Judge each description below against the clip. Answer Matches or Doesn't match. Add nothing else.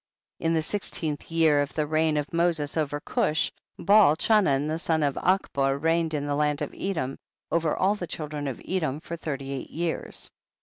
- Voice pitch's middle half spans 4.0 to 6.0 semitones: Doesn't match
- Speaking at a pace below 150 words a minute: Doesn't match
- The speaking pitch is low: Doesn't match